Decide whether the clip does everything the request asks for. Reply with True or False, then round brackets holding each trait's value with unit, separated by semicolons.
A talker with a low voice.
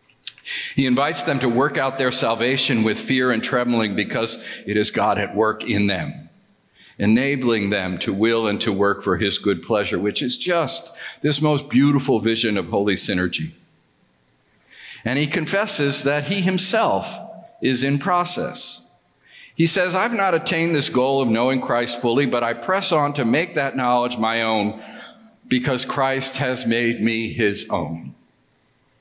True (125 Hz)